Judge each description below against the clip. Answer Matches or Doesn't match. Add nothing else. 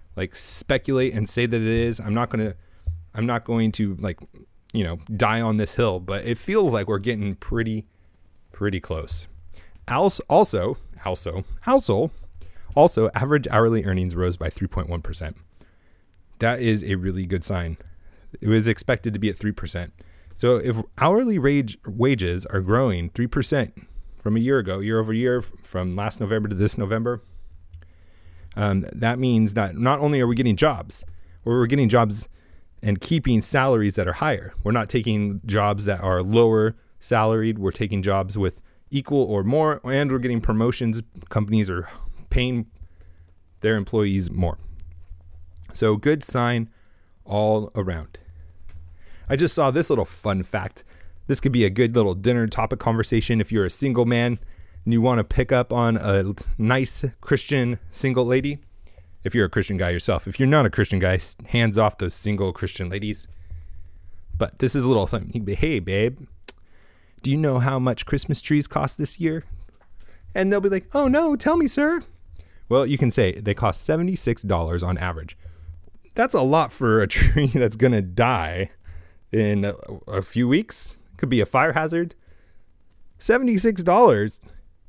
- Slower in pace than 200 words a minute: Matches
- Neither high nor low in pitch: Doesn't match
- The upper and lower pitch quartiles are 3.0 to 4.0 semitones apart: Doesn't match